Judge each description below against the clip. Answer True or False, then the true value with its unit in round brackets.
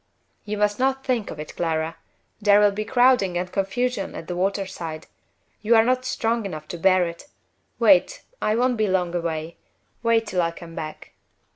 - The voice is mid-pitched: False (195 Hz)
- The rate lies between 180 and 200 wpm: True (185 wpm)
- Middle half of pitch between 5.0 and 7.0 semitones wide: True (5.3 semitones)